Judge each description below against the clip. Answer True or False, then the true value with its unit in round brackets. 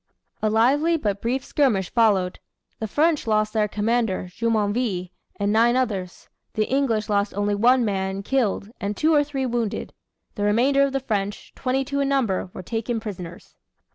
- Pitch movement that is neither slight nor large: True (4.2 semitones)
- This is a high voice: True (220 Hz)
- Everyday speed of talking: True (170 wpm)